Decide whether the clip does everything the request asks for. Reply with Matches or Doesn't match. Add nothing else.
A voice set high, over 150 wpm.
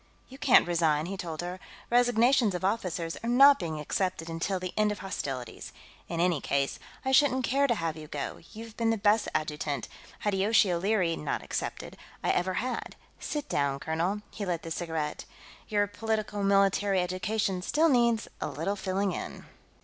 Matches